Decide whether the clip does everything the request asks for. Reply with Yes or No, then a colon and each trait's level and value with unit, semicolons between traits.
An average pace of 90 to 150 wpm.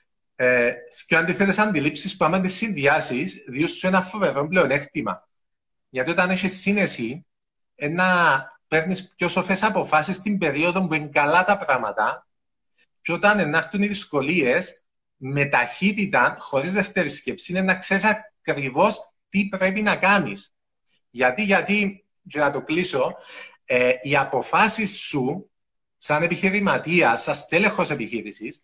Yes: average, 130 wpm